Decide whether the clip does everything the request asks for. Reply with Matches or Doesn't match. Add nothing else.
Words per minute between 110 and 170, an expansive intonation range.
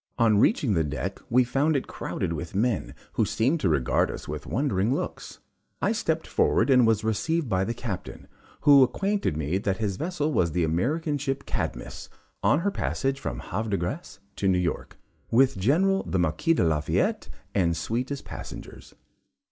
Doesn't match